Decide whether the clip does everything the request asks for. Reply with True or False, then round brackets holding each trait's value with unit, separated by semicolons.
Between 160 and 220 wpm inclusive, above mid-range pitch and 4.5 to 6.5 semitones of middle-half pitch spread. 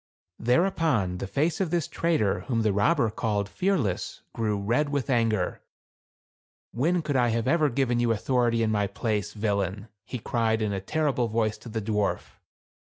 False (175 wpm; 115 Hz; 5.0 semitones)